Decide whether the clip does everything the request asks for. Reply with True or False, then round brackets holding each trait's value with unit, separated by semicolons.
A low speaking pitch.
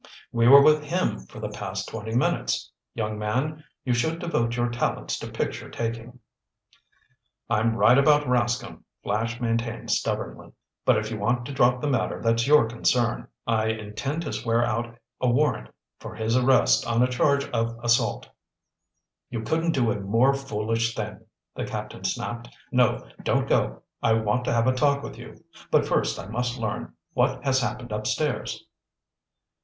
True (120 Hz)